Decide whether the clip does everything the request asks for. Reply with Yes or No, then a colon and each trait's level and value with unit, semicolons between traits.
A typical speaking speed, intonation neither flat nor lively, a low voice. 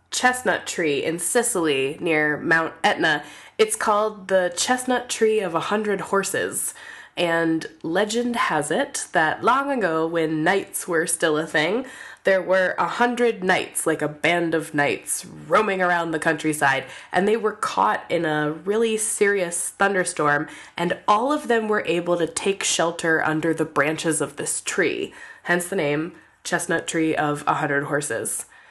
No: average, 160 wpm; average, 4.8 semitones; medium, 175 Hz